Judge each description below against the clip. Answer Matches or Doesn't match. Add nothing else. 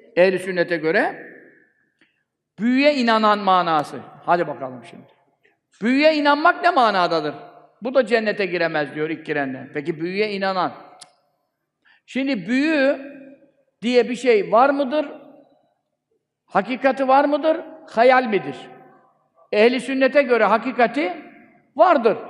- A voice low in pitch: Doesn't match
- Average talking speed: Matches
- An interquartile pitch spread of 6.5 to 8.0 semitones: Matches